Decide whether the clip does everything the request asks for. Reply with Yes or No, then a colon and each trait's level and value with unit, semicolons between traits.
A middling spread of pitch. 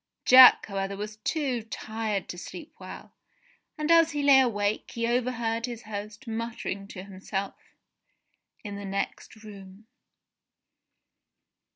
Yes: average, 3.5 semitones